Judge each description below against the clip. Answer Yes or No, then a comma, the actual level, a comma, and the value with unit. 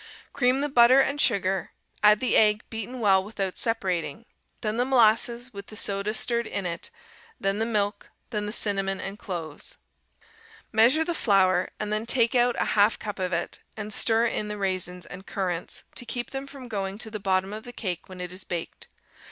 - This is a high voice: Yes, high, 210 Hz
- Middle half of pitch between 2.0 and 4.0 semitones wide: Yes, average, 3.6 semitones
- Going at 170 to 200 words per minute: Yes, average, 195 wpm